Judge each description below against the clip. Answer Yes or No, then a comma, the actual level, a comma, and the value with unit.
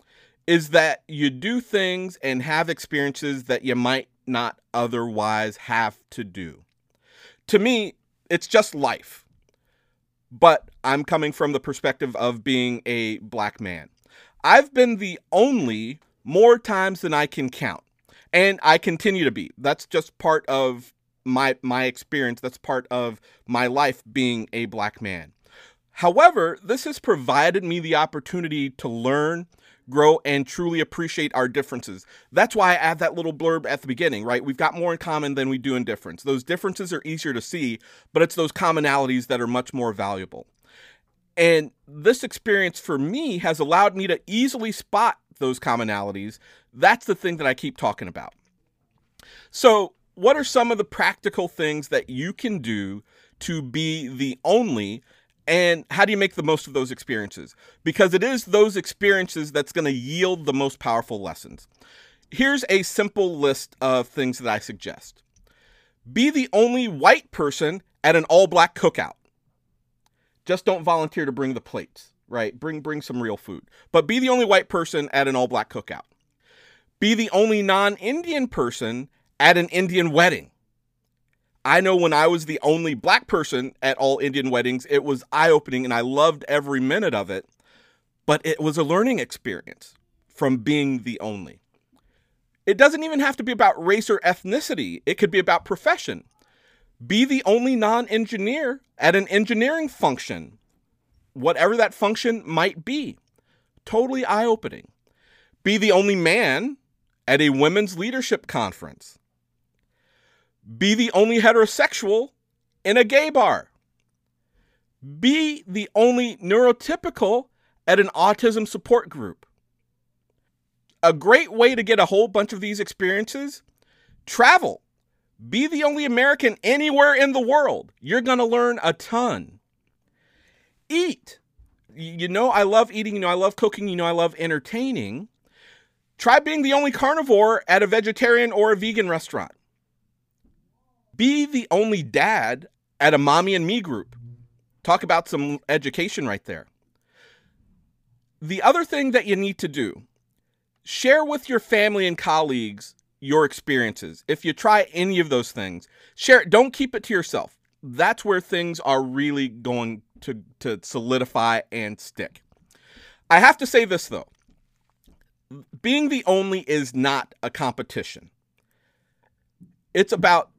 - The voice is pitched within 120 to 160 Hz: No, medium, 170 Hz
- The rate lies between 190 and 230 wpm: No, average, 155 wpm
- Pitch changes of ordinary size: No, wide, 8.8 semitones